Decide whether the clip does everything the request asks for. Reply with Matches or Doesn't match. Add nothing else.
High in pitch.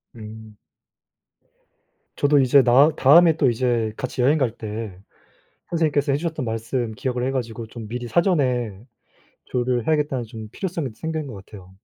Doesn't match